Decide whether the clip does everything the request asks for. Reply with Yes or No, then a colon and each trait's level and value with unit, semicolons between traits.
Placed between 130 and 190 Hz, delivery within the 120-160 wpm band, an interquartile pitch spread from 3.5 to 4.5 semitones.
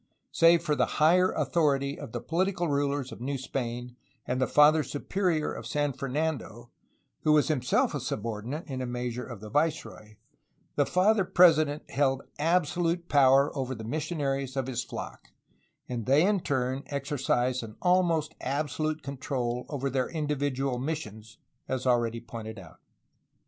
Yes: medium, 140 Hz; average, 150 wpm; average, 3.8 semitones